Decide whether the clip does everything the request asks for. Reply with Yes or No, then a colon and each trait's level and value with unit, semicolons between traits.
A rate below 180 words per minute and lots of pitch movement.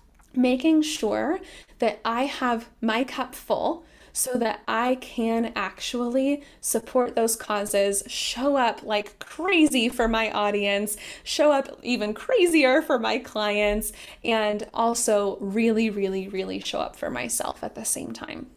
No: average, 140 wpm; average, 3.9 semitones